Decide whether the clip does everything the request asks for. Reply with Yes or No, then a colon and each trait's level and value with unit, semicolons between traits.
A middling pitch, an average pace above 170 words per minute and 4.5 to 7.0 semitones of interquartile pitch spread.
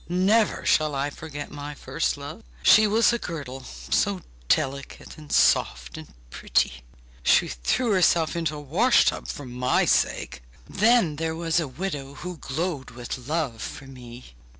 No: medium, 150 Hz; average, 155 wpm; average, 5.2 semitones